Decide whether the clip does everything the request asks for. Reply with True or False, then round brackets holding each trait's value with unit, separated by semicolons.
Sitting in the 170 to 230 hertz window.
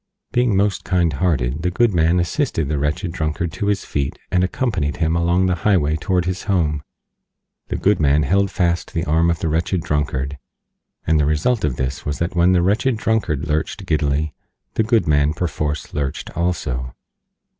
False (85 Hz)